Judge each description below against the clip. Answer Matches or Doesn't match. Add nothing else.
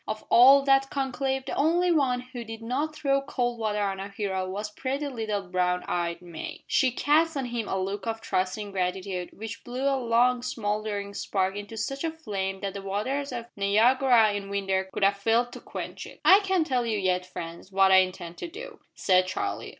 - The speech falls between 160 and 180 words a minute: Doesn't match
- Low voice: Doesn't match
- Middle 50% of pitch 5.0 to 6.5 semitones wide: Matches